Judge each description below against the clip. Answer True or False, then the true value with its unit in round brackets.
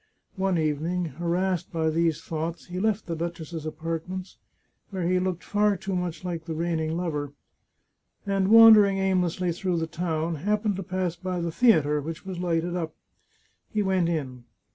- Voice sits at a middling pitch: True (175 Hz)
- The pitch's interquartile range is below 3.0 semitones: True (2.6 semitones)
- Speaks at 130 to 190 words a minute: True (165 wpm)